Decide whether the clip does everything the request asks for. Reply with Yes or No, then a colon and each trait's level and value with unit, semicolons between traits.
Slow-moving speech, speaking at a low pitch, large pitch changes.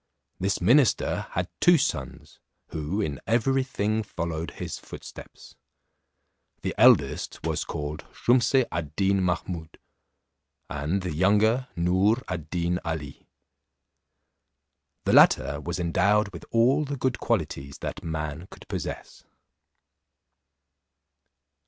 Yes: slow, 110 wpm; very low, 95 Hz; wide, 6.4 semitones